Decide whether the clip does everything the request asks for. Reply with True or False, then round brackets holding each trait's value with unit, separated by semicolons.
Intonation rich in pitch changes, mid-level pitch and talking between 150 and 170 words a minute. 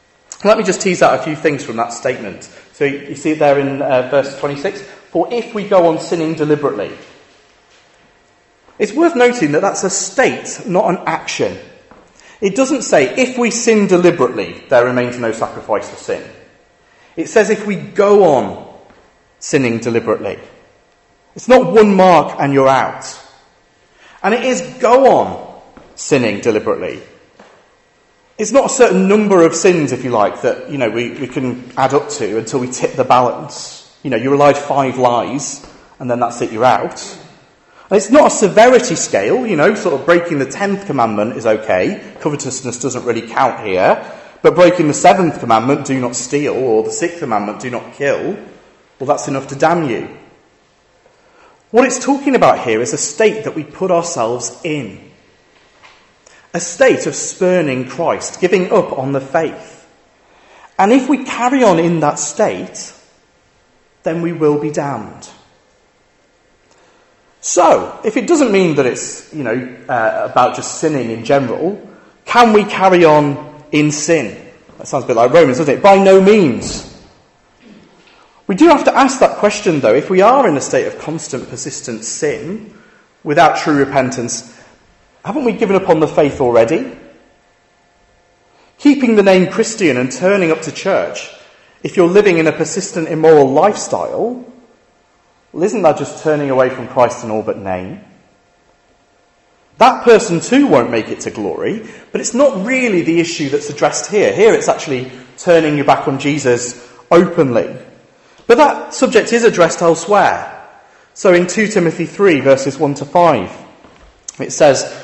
True (7.4 semitones; 170 Hz; 165 wpm)